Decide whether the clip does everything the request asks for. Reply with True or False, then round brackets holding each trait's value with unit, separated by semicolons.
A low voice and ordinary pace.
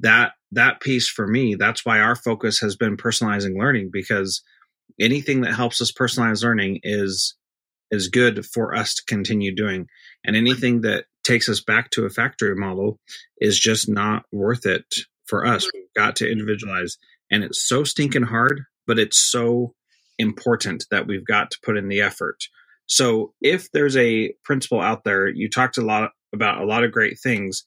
True (110 Hz; 180 wpm)